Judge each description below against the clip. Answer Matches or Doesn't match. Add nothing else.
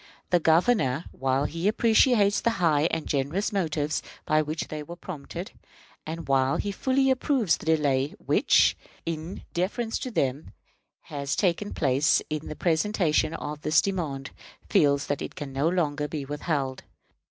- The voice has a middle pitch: Matches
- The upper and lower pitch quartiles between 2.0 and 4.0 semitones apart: Doesn't match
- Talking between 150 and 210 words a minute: Matches